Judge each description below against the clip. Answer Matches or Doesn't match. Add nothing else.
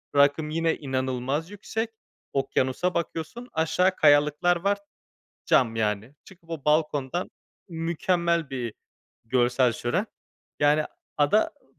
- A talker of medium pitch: Matches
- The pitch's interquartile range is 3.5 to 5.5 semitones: Matches